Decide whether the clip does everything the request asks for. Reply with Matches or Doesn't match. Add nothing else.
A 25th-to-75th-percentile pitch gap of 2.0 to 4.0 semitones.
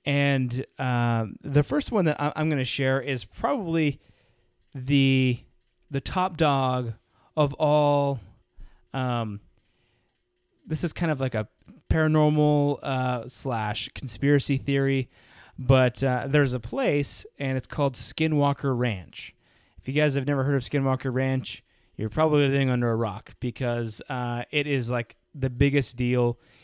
Matches